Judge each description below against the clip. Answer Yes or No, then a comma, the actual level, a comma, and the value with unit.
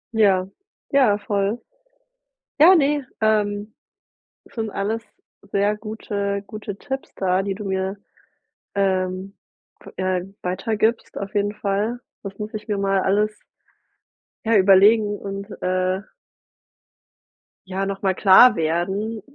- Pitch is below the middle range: No, high, 200 Hz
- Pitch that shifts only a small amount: Yes, narrow, 1.9 semitones